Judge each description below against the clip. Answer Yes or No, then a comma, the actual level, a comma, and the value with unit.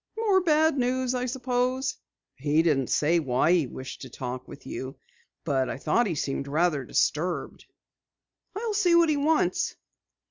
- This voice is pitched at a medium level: Yes, medium, 180 Hz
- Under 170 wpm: Yes, average, 155 wpm